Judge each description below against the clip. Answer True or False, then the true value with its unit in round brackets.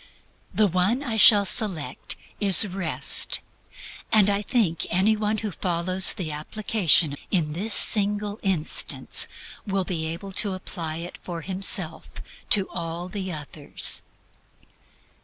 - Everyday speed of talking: False (125 wpm)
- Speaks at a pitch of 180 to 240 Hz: True (190 Hz)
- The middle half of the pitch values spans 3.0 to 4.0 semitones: True (3.6 semitones)